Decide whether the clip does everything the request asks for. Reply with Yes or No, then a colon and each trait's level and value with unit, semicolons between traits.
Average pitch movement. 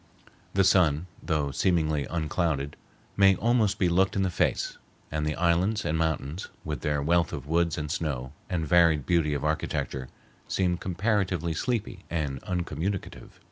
Yes: average, 3.5 semitones